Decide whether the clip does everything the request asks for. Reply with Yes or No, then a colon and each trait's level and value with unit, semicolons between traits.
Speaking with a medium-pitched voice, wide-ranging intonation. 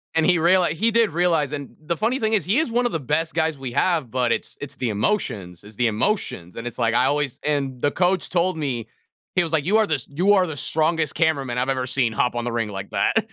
Yes: medium, 150 Hz; wide, 6.3 semitones